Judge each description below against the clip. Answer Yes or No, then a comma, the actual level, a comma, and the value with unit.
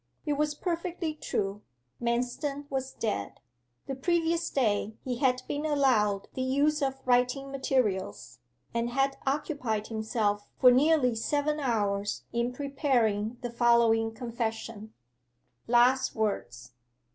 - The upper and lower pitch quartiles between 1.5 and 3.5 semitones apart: No, average, 4.0 semitones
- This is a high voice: Yes, very high, 250 Hz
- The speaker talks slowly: Yes, slow, 120 wpm